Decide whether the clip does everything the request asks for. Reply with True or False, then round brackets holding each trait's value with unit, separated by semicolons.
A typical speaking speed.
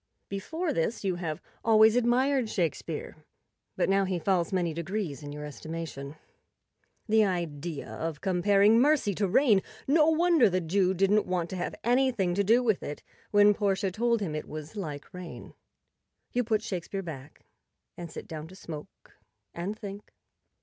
True (160 wpm)